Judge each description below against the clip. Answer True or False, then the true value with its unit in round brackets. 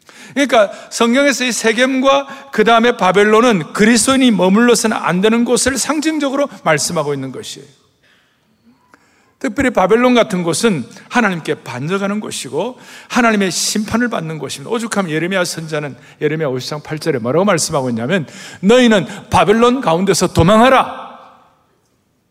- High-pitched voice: True (215 Hz)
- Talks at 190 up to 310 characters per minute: False (340 characters per minute)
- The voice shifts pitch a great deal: True (6.7 semitones)